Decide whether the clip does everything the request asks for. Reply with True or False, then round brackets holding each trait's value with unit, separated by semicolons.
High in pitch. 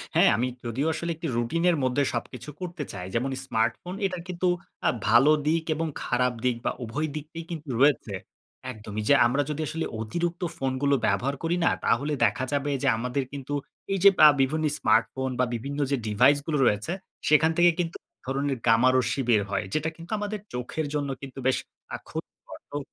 False (140 Hz)